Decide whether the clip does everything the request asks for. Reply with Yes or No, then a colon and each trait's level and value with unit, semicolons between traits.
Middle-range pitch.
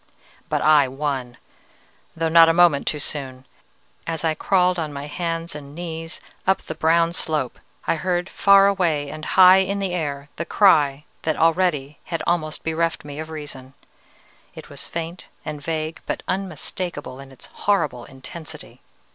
Yes: medium, 160 Hz